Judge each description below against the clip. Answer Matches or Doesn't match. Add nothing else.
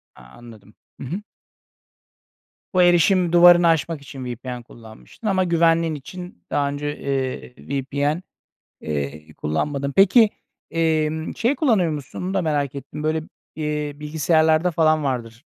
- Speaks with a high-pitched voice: Doesn't match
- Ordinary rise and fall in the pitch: Matches